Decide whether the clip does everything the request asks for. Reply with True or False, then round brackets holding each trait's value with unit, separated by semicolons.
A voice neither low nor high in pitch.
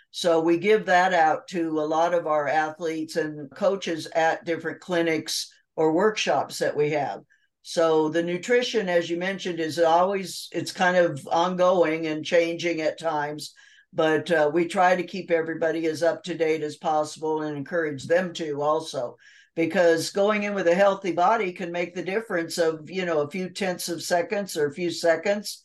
True (170 Hz)